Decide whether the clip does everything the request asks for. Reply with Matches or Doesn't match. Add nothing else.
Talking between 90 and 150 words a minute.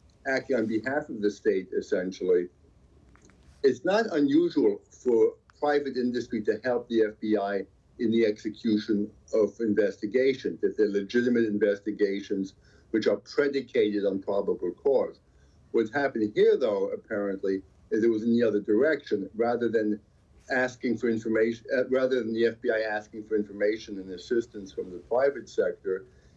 Matches